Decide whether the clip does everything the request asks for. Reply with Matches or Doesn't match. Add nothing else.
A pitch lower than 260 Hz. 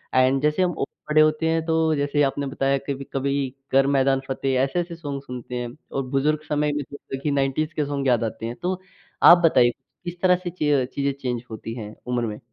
Matches